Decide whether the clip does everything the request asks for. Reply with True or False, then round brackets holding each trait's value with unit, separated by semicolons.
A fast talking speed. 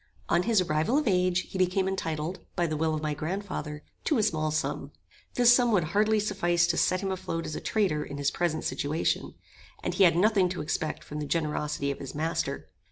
True (220 wpm)